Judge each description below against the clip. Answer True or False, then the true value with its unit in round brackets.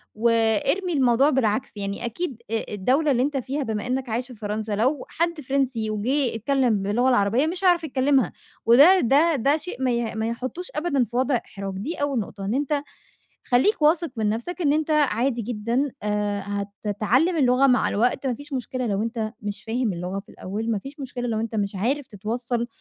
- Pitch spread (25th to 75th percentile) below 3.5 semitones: False (4.5 semitones)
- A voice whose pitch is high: True (245 Hz)